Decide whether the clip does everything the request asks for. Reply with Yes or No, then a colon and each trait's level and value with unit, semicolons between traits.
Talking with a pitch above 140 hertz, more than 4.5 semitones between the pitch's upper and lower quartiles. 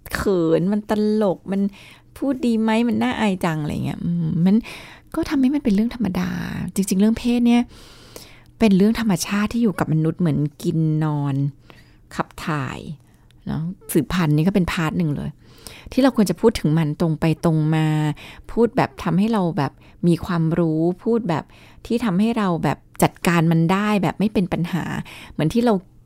Yes: medium, 185 Hz; average, 5.2 semitones